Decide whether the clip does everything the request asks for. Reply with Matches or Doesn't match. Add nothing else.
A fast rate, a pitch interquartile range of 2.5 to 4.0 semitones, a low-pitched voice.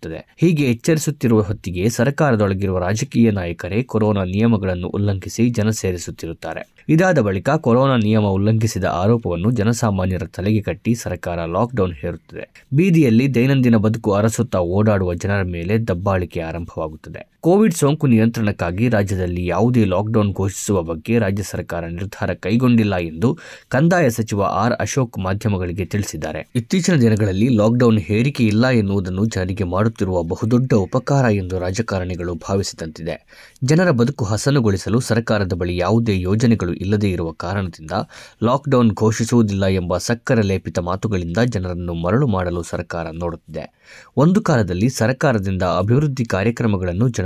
Doesn't match